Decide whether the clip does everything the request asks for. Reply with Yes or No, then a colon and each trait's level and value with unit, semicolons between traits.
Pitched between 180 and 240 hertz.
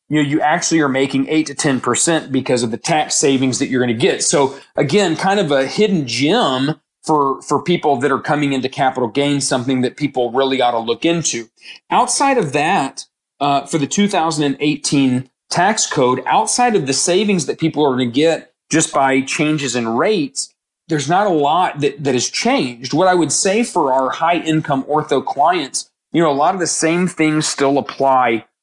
No: medium, 145 Hz